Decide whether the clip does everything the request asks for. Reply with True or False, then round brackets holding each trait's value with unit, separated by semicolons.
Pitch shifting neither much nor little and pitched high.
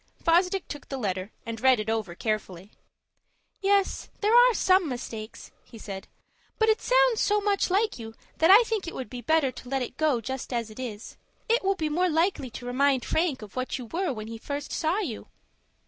False (8.9 semitones; 275 Hz)